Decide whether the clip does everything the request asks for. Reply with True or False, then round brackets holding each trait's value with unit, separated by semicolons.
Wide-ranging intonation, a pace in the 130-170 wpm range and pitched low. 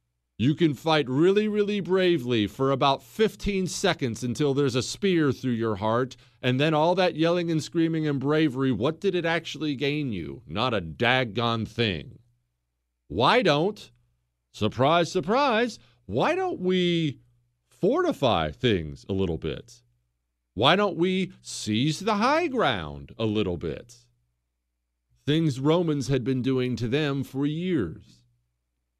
True (8.7 semitones; 140 wpm; 130 Hz)